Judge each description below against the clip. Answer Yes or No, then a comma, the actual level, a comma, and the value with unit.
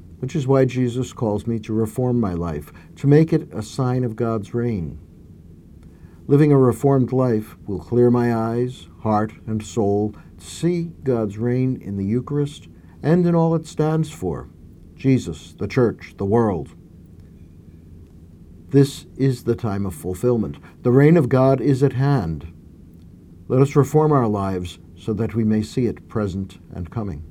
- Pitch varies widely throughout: Yes, wide, 7.2 semitones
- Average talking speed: Yes, average, 165 wpm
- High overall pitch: No, low, 110 Hz